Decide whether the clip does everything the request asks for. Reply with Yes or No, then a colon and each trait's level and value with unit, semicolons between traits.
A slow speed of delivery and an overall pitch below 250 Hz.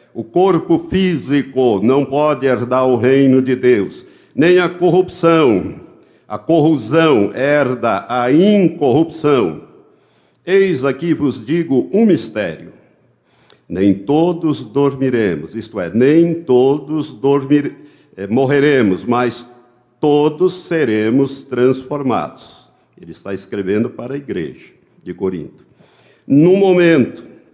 Yes: slow, 105 wpm; medium, 140 Hz